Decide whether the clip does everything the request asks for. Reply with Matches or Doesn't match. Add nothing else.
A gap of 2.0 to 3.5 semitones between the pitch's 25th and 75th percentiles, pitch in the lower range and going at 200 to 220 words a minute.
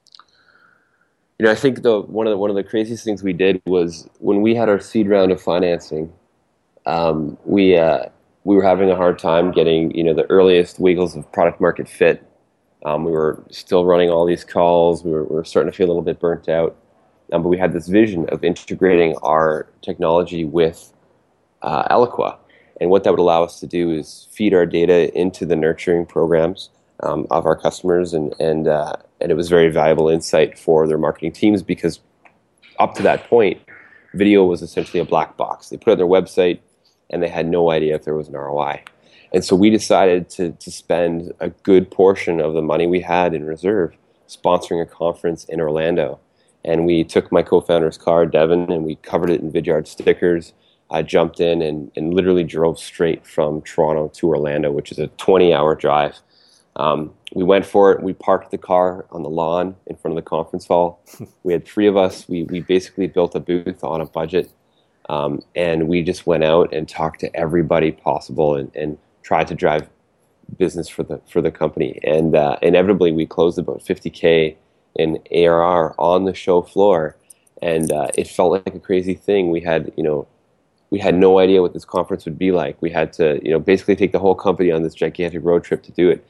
Matches